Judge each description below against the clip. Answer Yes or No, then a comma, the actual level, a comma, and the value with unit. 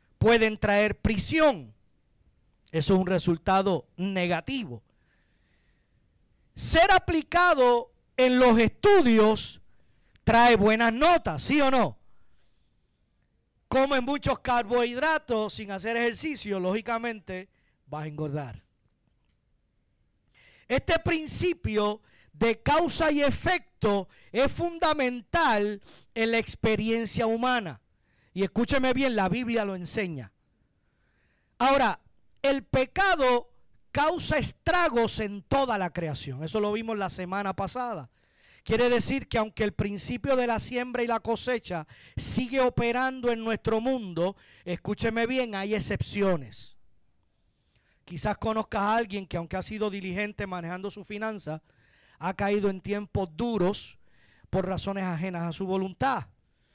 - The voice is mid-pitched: No, high, 215 Hz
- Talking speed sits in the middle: No, slow, 115 wpm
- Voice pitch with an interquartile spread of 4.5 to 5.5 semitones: Yes, average, 5.2 semitones